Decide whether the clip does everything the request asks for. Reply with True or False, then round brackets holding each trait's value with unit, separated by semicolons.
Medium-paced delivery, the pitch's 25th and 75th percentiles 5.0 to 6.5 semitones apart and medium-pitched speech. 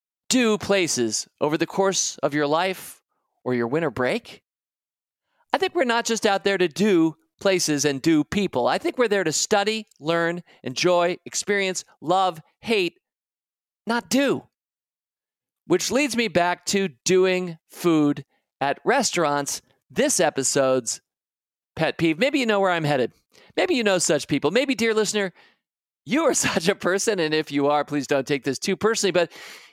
True (165 wpm; 5.6 semitones; 180 Hz)